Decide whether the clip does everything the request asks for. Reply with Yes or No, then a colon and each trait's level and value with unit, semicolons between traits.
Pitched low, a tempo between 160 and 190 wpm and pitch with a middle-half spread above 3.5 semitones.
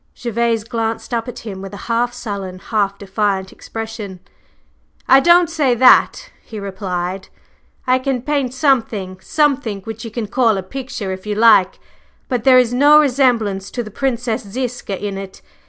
No: high, 225 Hz; average, 165 wpm; average, 4.3 semitones